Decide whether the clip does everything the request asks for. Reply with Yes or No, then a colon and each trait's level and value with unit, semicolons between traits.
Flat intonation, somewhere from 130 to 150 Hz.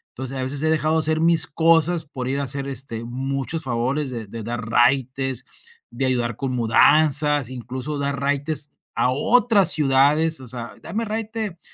No: average, 3.7 semitones; medium, 140 Hz